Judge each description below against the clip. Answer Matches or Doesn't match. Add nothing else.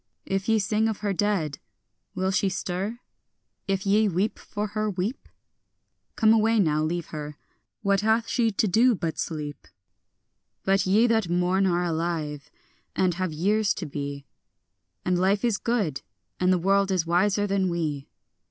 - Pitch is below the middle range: Doesn't match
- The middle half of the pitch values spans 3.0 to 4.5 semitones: Matches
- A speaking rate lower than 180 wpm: Matches